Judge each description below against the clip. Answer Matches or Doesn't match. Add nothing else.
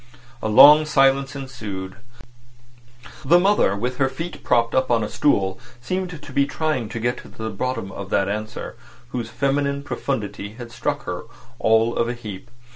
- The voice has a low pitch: Matches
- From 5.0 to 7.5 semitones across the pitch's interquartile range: Doesn't match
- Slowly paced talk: Doesn't match